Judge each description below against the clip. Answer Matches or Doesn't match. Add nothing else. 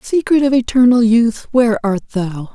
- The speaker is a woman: Matches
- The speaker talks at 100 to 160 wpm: Matches